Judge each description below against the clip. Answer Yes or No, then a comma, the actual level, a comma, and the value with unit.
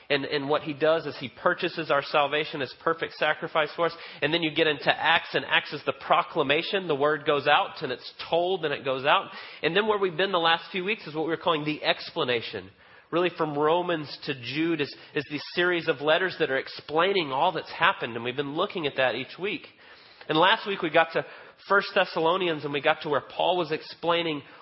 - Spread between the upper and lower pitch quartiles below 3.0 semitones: Yes, narrow, 2.5 semitones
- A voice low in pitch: No, medium, 160 Hz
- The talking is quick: Yes, fast, 230 wpm